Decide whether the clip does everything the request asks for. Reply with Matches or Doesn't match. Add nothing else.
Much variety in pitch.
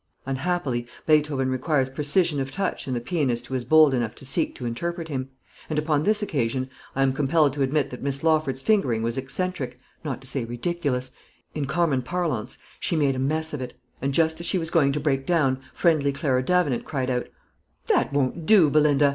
Doesn't match